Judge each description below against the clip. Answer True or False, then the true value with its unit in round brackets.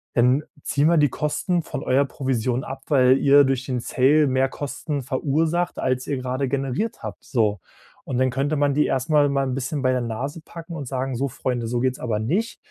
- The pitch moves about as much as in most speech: False (2.2 semitones)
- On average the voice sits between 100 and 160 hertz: True (135 Hz)